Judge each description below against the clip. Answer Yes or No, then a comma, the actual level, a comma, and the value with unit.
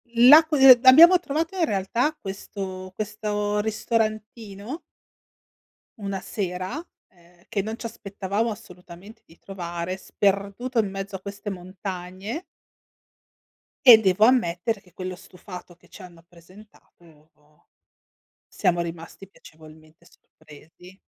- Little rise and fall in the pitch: No, average, 3.5 semitones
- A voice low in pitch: No, high, 195 Hz